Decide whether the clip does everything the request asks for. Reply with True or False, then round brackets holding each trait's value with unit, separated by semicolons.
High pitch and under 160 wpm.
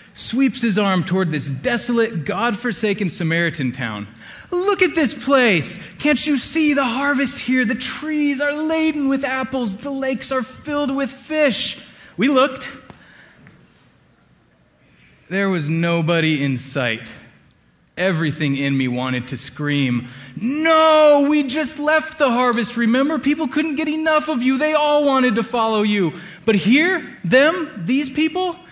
True (245 Hz; 145 wpm)